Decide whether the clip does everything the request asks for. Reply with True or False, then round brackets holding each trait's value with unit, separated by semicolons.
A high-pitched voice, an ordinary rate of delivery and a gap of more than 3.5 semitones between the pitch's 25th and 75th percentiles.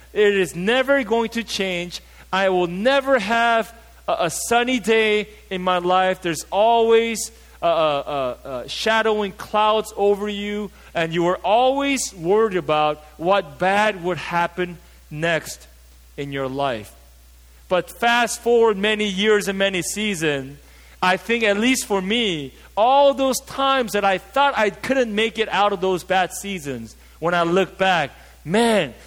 True (200 Hz; 155 wpm; 4.5 semitones)